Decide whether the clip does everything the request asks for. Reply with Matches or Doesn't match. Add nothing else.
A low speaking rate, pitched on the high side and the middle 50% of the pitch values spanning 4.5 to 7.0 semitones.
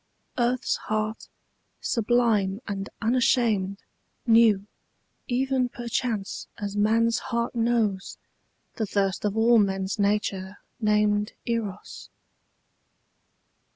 Doesn't match